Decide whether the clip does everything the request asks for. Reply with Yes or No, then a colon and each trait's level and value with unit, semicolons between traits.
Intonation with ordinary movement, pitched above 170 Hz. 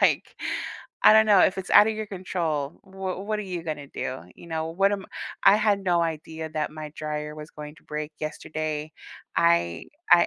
No: average, 4.0 semitones; medium, 160 Hz